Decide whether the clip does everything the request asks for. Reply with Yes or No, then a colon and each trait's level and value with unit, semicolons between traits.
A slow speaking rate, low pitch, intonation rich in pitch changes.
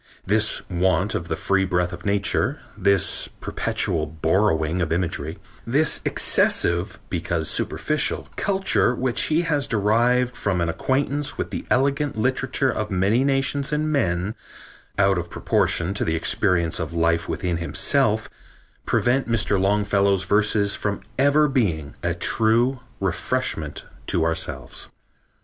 Yes: slow, 130 wpm; low, 100 Hz; wide, 6.9 semitones